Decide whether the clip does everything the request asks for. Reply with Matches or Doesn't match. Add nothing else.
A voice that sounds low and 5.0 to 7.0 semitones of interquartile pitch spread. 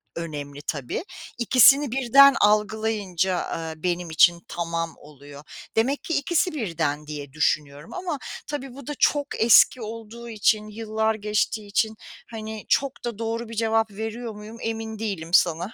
Doesn't match